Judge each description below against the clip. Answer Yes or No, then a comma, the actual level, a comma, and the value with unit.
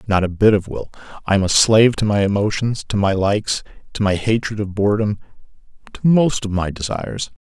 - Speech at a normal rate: Yes, average, 185 wpm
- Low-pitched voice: Yes, low, 105 Hz